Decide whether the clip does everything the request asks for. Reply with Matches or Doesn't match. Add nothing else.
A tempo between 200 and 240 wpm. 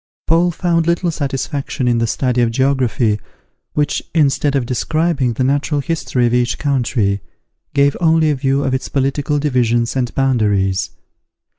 Doesn't match